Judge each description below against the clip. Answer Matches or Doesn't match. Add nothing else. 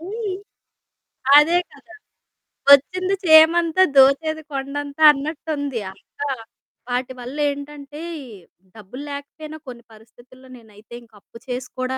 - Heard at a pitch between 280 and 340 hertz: Matches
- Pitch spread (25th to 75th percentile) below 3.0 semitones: Doesn't match